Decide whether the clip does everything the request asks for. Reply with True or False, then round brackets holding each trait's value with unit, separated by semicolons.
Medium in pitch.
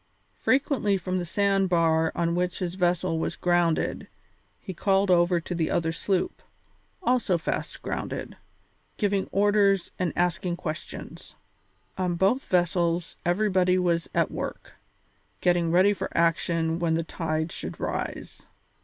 True (175 Hz)